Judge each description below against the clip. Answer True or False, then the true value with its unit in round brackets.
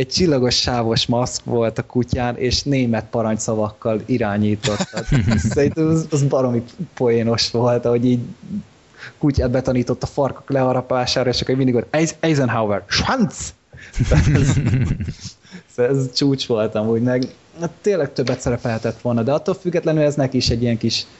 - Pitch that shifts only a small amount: False (3.2 semitones)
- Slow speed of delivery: False (140 wpm)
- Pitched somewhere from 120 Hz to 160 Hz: True (125 Hz)